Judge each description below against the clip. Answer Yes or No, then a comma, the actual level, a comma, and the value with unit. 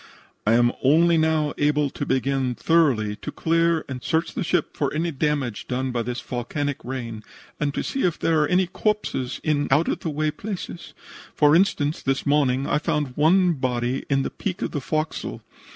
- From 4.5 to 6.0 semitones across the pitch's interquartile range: No, average, 3.8 semitones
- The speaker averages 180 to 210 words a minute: Yes, average, 190 wpm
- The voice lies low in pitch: No, medium, 150 Hz